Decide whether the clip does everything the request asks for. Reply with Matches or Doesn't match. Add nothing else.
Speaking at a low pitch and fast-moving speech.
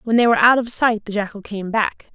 Doesn't match